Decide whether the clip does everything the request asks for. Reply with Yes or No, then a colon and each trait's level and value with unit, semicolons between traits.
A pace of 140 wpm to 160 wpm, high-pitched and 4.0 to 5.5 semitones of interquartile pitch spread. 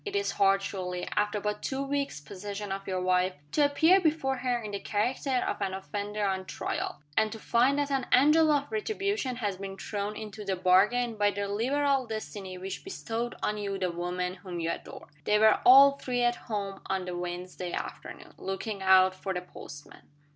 No: average, 195 wpm; high, 210 Hz; average, 5.1 semitones